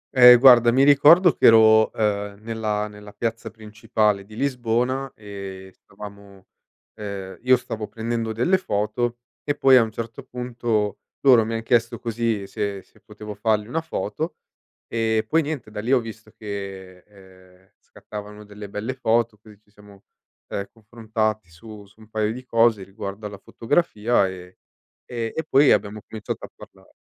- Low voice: Yes, low, 110 Hz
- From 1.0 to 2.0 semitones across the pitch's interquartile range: No, narrow, 2.5 semitones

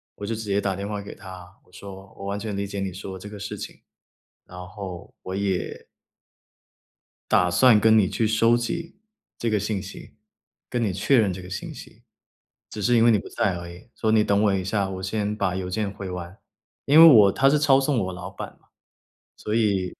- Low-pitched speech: Yes, low, 100 Hz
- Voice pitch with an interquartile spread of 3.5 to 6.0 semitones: No, average, 2.7 semitones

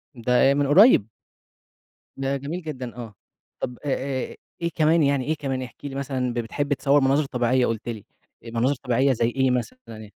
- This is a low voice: Yes, low, 130 Hz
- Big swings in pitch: No, average, 2.9 semitones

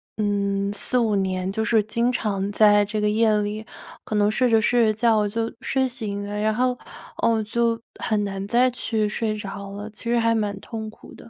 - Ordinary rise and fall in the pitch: No, narrow, 1.9 semitones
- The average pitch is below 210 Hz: No, high, 215 Hz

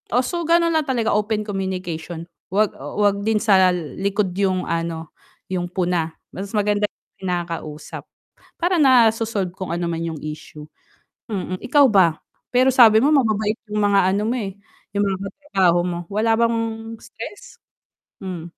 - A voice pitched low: No, high, 200 Hz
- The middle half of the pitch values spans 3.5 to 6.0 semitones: Yes, average, 4.1 semitones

